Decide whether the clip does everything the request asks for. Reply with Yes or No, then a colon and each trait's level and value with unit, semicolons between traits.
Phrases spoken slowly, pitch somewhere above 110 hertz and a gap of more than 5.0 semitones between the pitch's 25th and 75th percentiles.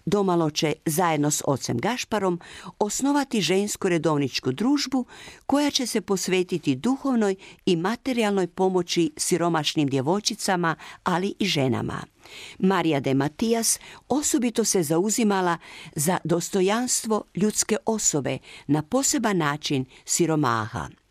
Yes: slow, 105 wpm; medium, 185 Hz; wide, 5.5 semitones